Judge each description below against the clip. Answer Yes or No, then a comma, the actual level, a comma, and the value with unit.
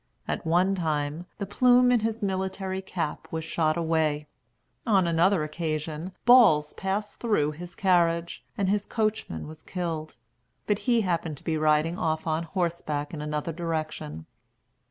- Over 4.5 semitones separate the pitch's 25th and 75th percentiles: No, average, 3.7 semitones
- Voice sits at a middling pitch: Yes, medium, 170 Hz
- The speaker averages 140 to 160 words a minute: Yes, average, 150 wpm